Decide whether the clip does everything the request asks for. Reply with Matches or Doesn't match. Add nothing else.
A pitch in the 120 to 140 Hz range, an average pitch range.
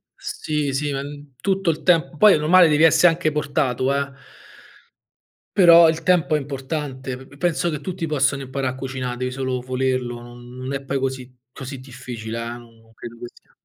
Matches